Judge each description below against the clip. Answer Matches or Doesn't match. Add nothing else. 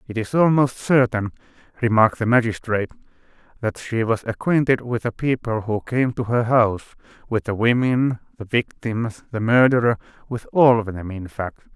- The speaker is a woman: Doesn't match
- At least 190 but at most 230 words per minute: Doesn't match